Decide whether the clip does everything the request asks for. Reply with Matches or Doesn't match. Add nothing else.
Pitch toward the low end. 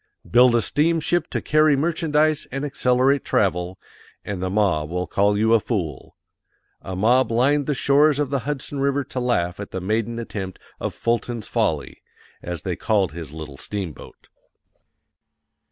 Matches